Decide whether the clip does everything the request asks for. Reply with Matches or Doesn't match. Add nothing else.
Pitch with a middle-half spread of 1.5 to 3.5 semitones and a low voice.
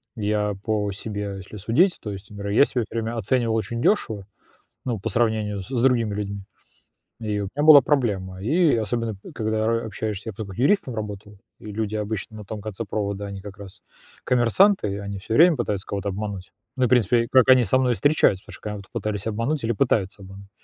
Matches